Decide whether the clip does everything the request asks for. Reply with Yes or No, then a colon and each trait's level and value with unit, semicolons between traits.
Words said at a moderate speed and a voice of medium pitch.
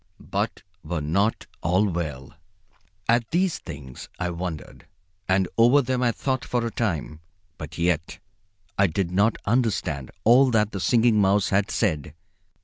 No: average, 145 wpm; low, 100 Hz